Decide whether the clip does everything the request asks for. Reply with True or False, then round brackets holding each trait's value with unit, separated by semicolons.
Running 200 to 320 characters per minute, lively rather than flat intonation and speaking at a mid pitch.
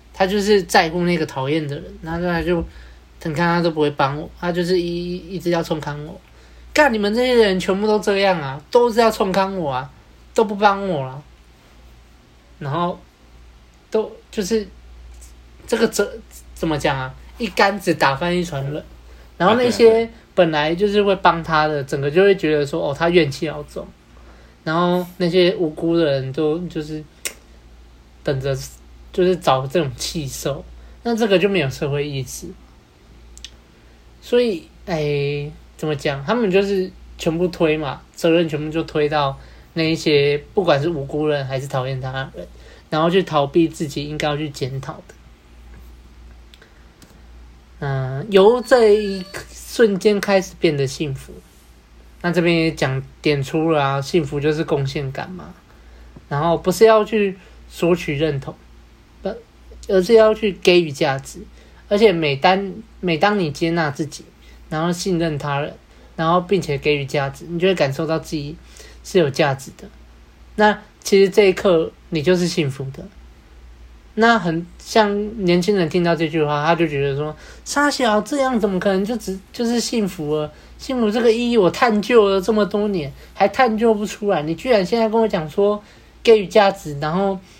True (240 characters per minute; 5.9 semitones; 165 Hz)